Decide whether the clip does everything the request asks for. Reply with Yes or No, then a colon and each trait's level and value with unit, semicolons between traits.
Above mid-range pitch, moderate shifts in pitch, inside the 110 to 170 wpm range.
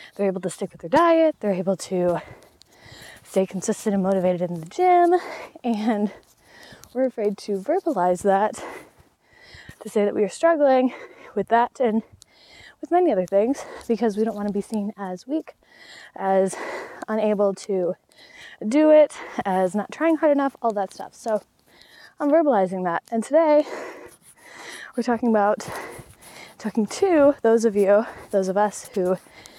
No: high, 215 Hz; wide, 6.4 semitones; average, 155 wpm